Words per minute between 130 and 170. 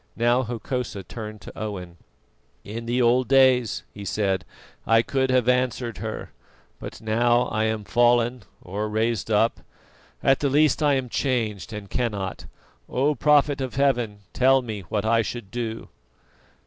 Yes: average, 150 wpm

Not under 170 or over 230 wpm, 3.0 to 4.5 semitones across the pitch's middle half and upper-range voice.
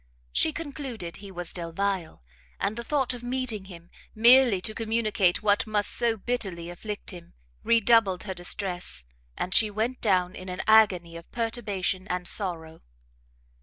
No: average, 150 wpm; average, 4.2 semitones; high, 200 Hz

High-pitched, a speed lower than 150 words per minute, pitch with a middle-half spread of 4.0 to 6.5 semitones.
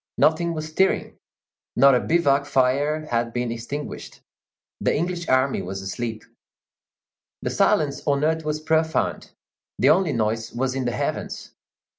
No: medium, 140 Hz; average, 140 wpm; average, 4.6 semitones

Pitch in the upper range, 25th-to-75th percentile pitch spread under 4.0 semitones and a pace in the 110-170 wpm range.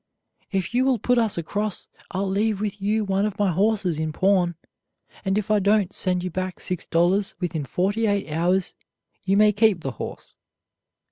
No: high, 195 Hz; average, 2.7 semitones; average, 185 wpm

